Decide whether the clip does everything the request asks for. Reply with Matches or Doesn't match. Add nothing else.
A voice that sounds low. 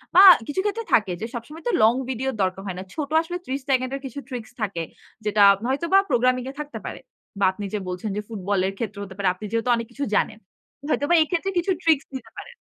Doesn't match